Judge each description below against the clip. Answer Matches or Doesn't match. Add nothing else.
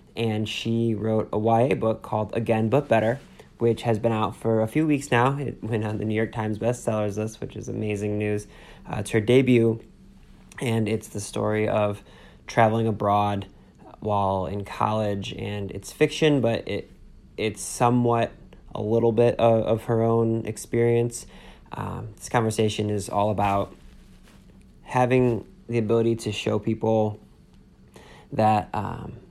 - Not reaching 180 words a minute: Matches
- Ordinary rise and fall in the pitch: Doesn't match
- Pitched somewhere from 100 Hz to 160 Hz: Matches